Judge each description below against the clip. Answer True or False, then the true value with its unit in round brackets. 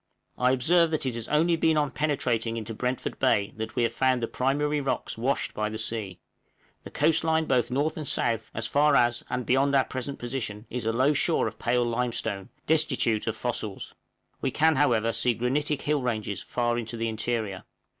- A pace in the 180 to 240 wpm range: True (195 wpm)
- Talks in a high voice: False (125 Hz)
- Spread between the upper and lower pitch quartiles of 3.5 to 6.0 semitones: True (3.9 semitones)